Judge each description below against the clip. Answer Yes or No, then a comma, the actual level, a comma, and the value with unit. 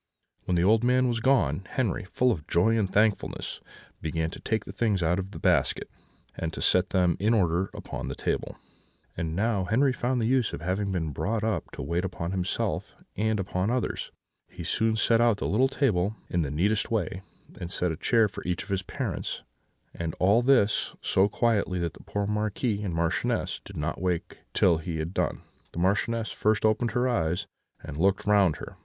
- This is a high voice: No, low, 100 Hz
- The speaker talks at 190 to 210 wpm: Yes, average, 200 wpm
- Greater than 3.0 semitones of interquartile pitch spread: Yes, average, 4.2 semitones